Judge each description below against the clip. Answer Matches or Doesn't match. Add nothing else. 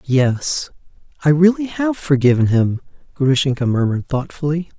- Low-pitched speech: Doesn't match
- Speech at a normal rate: Doesn't match